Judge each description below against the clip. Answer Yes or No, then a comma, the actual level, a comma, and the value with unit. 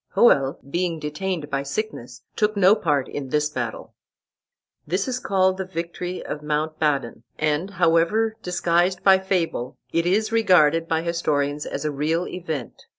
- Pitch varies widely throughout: No, average, 4.0 semitones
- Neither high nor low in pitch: Yes, medium, 165 Hz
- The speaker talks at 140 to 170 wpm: Yes, average, 150 wpm